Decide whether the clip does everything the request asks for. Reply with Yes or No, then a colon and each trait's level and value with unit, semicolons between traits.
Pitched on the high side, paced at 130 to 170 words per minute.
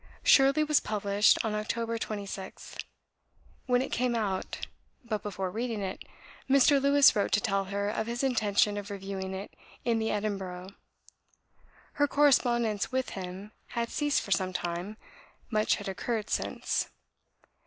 Yes: high, 215 Hz; average, 145 wpm